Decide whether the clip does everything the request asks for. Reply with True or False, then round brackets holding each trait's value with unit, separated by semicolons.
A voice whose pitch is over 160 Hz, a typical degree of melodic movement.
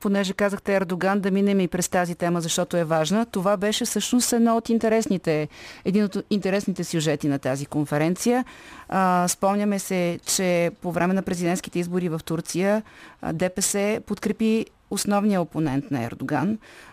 True (190 Hz; 3.1 semitones)